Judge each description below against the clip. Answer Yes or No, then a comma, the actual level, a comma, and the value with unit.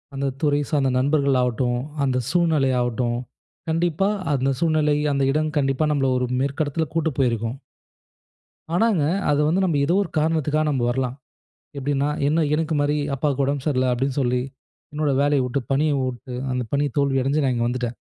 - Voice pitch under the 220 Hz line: Yes, medium, 140 Hz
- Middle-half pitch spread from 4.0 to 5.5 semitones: No, average, 3.0 semitones